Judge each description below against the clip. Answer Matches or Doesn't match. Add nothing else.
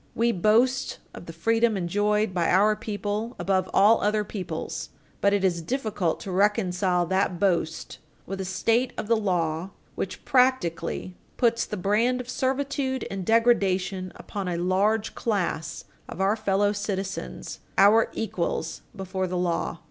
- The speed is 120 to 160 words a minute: Matches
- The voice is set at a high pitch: Matches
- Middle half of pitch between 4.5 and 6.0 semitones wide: Doesn't match